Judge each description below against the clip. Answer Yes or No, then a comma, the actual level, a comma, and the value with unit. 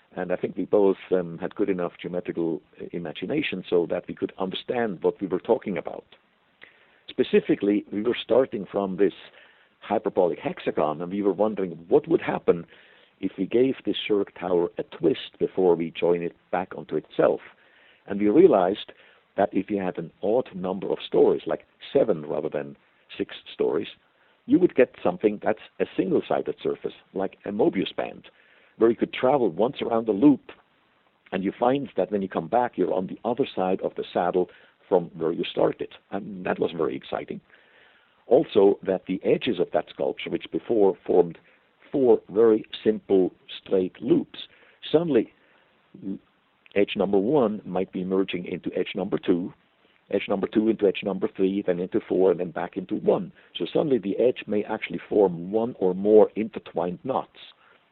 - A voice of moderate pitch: No, low, 105 Hz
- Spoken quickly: No, average, 175 wpm